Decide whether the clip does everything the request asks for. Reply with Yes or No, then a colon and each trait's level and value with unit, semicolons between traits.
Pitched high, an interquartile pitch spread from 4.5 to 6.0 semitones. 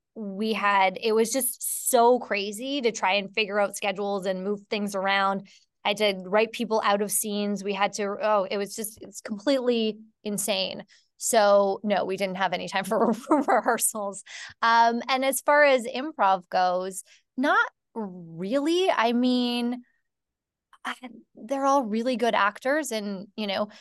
No: high, 215 Hz; average, 3.2 semitones